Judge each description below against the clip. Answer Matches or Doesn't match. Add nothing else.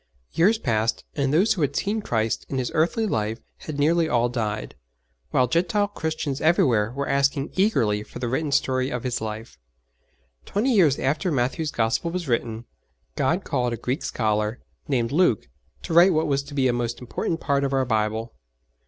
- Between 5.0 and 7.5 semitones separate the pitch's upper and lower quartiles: Matches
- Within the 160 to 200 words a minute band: Matches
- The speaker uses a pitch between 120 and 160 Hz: Matches